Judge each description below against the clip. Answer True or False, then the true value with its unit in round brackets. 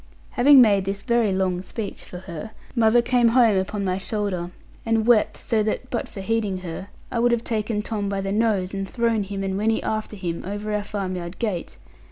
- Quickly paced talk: True (210 wpm)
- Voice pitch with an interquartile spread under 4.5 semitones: True (2.9 semitones)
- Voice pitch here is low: False (210 Hz)